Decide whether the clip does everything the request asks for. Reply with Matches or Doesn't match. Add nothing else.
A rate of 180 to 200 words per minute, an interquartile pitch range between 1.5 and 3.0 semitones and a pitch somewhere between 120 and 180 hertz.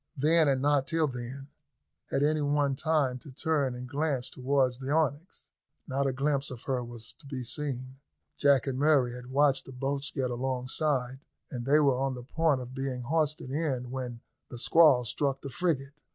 Matches